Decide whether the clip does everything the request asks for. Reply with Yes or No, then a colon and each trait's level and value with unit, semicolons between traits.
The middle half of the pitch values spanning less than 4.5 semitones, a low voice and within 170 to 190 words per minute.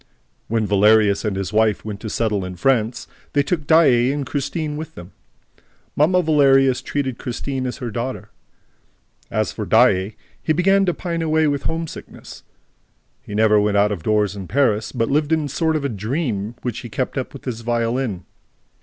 No: wide, 5.6 semitones; low, 125 Hz; average, 180 wpm